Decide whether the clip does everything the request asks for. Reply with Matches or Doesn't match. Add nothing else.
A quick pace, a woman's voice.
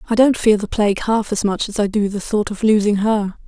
Matches